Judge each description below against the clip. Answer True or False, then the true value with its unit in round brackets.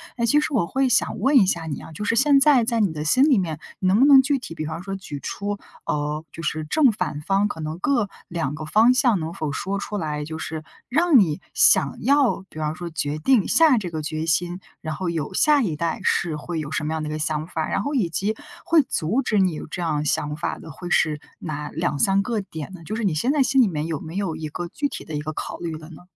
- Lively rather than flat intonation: True (6.5 semitones)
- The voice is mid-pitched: True (175 Hz)